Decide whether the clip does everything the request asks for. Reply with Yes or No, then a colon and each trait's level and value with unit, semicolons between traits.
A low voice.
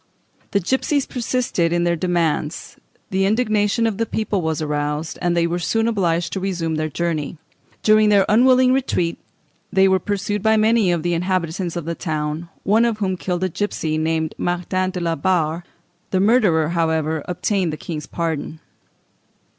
No: medium, 175 Hz